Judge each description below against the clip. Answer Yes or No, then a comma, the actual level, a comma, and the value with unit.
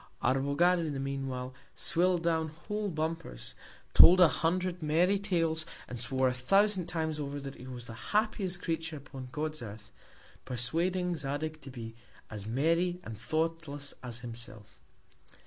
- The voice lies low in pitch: No, medium, 155 Hz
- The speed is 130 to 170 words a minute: Yes, average, 150 wpm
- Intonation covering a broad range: No, average, 5.0 semitones